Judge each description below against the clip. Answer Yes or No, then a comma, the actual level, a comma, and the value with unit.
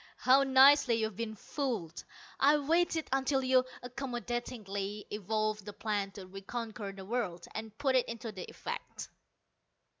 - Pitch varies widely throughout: No, average, 4.2 semitones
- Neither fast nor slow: No, slow, 130 wpm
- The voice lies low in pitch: No, high, 230 Hz